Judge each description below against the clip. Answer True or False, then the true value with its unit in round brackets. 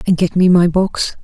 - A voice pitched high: False (180 Hz)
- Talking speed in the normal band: False (245 wpm)